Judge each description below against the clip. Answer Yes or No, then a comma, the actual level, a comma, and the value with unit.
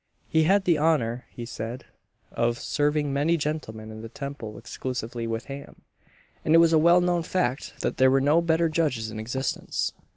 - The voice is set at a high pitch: No, medium, 140 Hz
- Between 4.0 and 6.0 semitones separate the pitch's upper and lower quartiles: Yes, wide, 5.5 semitones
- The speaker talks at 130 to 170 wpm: No, average, 185 wpm